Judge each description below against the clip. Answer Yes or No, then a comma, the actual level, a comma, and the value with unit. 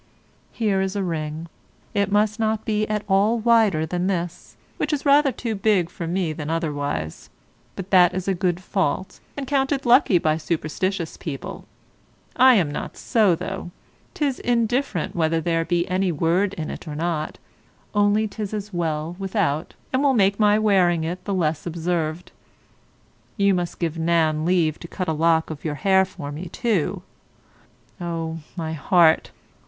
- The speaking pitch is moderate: Yes, medium, 180 Hz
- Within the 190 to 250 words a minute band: No, average, 165 wpm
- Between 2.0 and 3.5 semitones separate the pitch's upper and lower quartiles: No, average, 4.2 semitones